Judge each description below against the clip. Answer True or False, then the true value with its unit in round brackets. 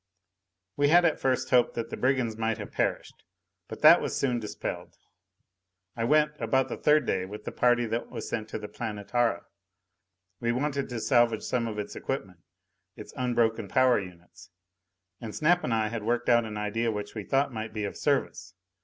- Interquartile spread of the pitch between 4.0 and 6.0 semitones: False (3.2 semitones)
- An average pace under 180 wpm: False (190 wpm)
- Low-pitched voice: True (115 Hz)